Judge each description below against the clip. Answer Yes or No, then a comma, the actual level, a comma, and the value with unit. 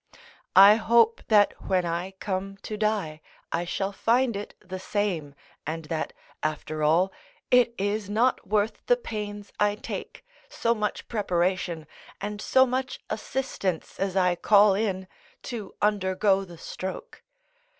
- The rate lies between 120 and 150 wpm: Yes, average, 140 wpm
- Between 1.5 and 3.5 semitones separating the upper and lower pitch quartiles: Yes, average, 2.7 semitones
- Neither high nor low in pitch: No, high, 200 Hz